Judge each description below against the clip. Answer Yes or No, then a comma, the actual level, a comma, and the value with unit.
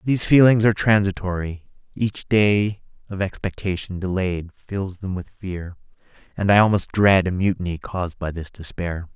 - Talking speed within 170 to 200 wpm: No, average, 150 wpm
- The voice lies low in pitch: Yes, very low, 95 Hz